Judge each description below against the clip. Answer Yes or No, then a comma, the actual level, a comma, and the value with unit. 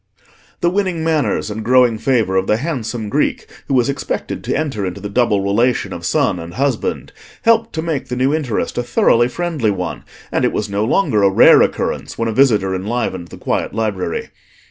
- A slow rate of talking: No, average, 195 wpm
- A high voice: No, low, 115 Hz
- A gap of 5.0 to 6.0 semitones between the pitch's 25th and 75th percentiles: Yes, wide, 5.5 semitones